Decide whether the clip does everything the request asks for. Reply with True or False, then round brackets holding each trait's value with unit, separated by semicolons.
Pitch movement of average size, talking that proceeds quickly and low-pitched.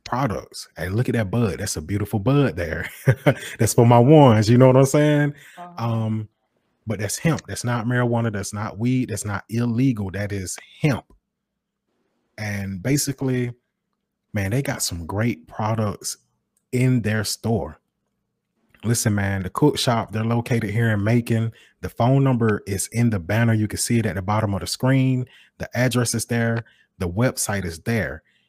False (3.4 semitones; 175 wpm; 115 Hz)